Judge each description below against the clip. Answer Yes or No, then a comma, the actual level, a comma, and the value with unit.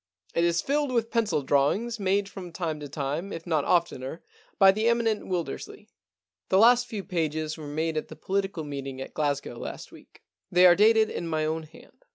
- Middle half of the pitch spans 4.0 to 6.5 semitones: Yes, average, 5.0 semitones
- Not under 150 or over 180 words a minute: No, average, 200 wpm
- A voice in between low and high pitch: Yes, medium, 170 Hz